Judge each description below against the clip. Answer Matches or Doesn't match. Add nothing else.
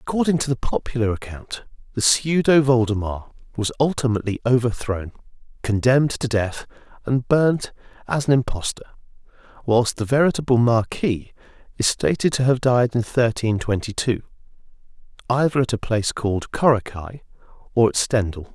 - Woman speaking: Doesn't match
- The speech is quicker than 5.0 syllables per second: Matches